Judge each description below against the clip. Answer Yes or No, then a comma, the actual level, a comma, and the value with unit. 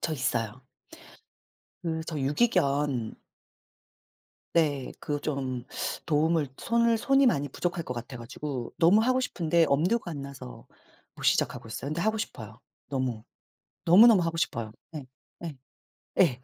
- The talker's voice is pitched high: No, medium, 150 Hz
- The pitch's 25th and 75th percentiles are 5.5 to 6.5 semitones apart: No, average, 5.1 semitones